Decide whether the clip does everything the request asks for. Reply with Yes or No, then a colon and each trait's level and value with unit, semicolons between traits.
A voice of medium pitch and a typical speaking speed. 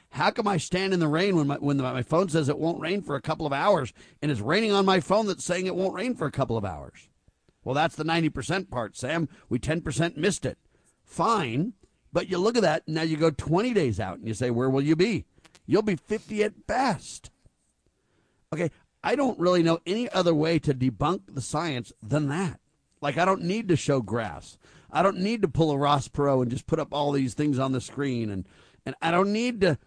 No: medium, 155 Hz; fast, 235 wpm